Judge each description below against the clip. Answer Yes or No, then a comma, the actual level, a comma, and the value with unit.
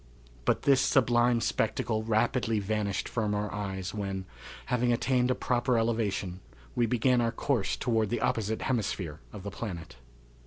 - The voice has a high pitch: No, low, 115 Hz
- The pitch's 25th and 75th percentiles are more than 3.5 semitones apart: No, average, 3.2 semitones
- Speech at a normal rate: Yes, average, 150 wpm